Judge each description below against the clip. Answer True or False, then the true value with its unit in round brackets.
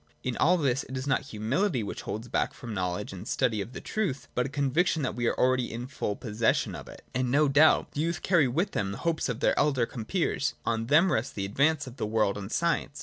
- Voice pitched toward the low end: True (130 Hz)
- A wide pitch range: False (4.8 semitones)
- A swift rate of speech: True (255 wpm)